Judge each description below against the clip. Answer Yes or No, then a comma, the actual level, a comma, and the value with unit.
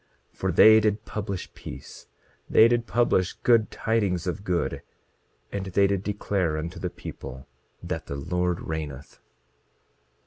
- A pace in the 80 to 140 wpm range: Yes, slow, 135 wpm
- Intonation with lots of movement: No, average, 3.9 semitones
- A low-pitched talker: Yes, very low, 95 Hz